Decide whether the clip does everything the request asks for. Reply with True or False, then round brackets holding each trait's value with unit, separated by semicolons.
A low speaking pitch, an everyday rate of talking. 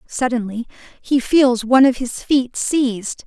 False (250 Hz; 145 wpm)